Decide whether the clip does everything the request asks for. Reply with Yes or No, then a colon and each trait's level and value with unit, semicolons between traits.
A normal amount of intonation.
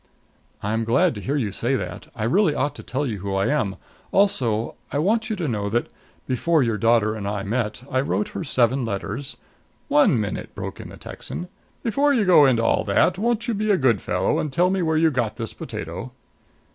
No: wide, 8.6 semitones